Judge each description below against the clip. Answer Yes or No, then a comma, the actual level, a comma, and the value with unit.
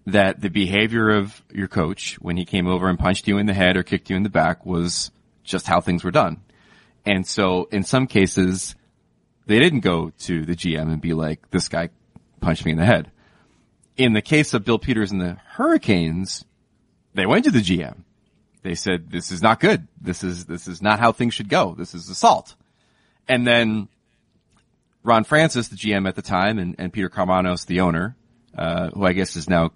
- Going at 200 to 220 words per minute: Yes, fast, 205 wpm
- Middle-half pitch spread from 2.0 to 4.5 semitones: Yes, average, 3.4 semitones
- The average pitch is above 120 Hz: No, very low, 95 Hz